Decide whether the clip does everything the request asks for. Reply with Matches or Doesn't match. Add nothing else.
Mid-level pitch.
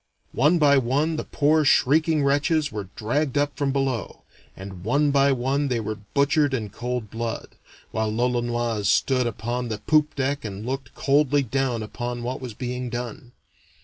Doesn't match